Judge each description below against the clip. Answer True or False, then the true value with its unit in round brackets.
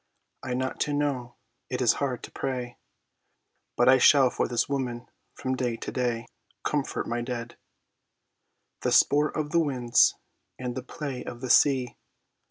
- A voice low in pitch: True (125 Hz)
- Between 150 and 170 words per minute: True (160 wpm)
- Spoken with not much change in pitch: True (2.3 semitones)